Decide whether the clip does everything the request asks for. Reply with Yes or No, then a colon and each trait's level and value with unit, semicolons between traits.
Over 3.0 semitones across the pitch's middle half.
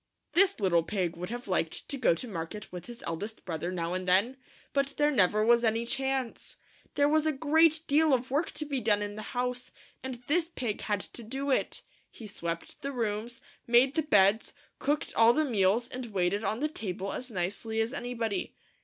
Yes: average, 5.2 semitones